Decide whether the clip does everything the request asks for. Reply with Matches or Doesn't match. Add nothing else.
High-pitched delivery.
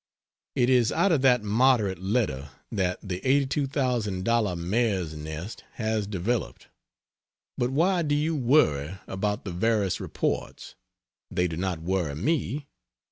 Doesn't match